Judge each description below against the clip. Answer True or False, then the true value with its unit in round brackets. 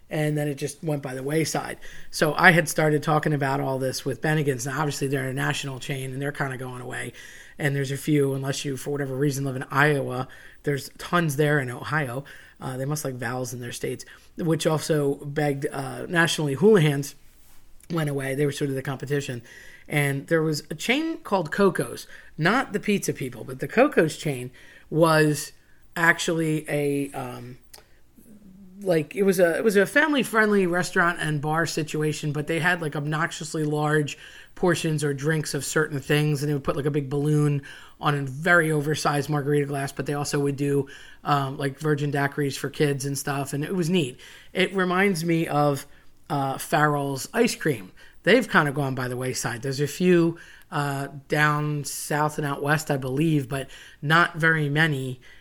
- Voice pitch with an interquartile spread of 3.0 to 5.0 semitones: False (2.5 semitones)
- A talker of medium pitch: True (150 Hz)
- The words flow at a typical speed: True (190 wpm)